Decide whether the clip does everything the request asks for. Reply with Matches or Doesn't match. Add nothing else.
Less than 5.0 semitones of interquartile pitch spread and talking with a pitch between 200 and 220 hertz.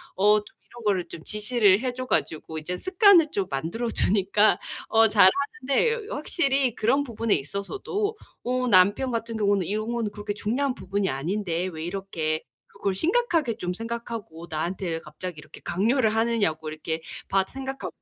Doesn't match